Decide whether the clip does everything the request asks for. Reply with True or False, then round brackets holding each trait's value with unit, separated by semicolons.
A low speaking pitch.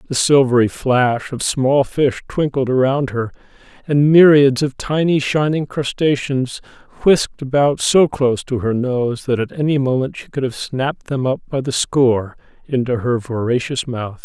True (130 Hz)